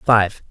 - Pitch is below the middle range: Yes, low, 105 Hz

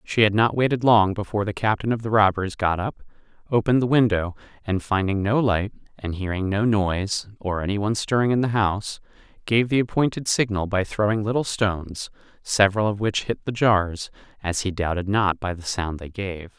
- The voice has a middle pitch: No, low, 100 Hz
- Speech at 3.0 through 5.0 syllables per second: No, 5.5 syllables/s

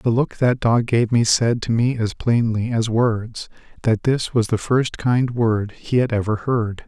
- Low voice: Yes, low, 115 Hz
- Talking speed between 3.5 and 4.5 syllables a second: Yes, 4.0 syllables/s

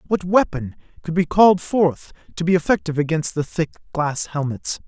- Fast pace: No, average, 170 wpm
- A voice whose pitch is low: No, medium, 165 Hz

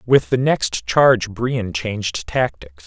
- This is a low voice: Yes, low, 110 Hz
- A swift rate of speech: No, average, 145 wpm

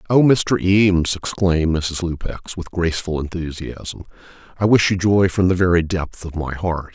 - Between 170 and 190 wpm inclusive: Yes, average, 175 wpm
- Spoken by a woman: No, male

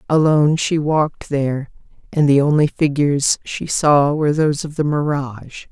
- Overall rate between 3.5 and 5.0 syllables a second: No, 5.2 syllables/s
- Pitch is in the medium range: Yes, medium, 145 Hz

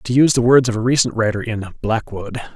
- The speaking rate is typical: No, fast, 235 wpm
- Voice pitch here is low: Yes, low, 115 Hz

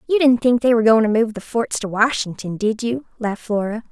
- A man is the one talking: No, female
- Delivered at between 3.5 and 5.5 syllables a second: No, 5.9 syllables/s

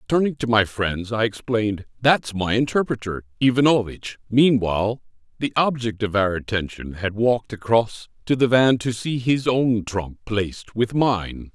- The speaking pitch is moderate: No, low, 115 Hz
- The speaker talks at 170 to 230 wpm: No, average, 155 wpm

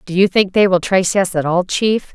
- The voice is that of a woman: Yes, female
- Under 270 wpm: No, fast, 280 wpm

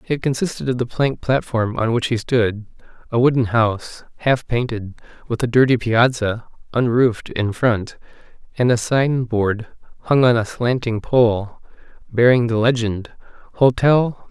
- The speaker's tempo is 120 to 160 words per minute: Yes, average, 145 wpm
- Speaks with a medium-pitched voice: No, low, 120 Hz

